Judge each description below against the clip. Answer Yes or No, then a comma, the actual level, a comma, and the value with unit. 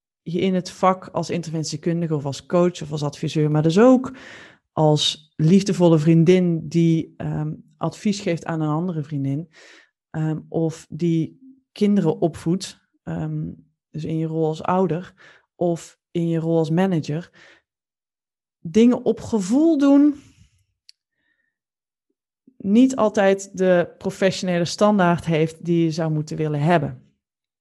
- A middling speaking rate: No, slow, 130 wpm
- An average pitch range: Yes, average, 3.4 semitones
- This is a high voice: No, medium, 165 Hz